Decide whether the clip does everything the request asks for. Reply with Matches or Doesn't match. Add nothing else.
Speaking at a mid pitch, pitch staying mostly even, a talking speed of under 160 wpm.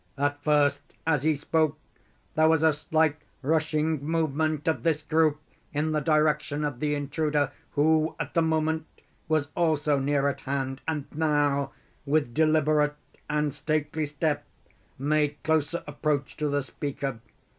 Matches